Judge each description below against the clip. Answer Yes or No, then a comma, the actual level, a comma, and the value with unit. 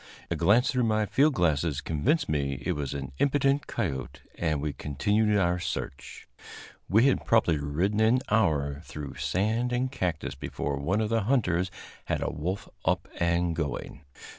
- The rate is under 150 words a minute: No, average, 165 wpm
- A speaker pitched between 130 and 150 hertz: No, very low, 90 Hz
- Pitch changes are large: Yes, wide, 7.3 semitones